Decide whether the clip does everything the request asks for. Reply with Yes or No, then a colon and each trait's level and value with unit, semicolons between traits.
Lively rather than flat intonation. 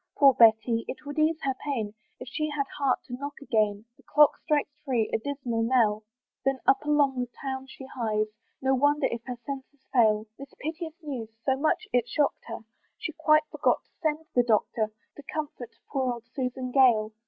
No: average, 3.8 semitones